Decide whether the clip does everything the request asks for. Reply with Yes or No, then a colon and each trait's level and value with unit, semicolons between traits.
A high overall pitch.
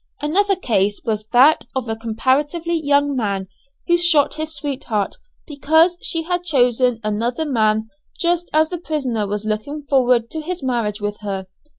Yes: very high, 265 Hz